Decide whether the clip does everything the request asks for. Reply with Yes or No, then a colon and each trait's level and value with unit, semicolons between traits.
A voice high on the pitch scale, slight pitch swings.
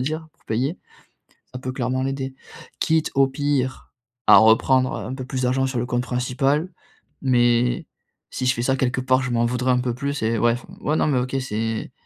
No: low, 130 Hz; narrow, 1.6 semitones